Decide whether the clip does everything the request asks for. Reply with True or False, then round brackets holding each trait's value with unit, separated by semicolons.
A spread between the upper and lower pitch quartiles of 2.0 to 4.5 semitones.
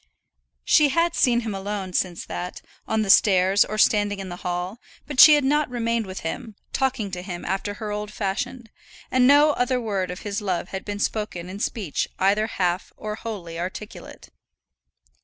True (3.8 semitones)